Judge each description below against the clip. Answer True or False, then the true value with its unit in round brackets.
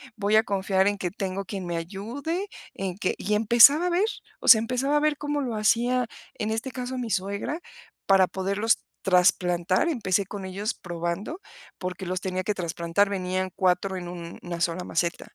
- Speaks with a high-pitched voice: True (195 Hz)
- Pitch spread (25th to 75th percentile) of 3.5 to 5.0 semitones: True (4.0 semitones)